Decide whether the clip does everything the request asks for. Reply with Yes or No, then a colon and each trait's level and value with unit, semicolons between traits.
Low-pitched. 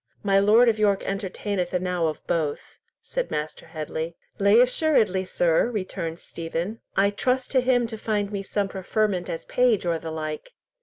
No: high, 195 Hz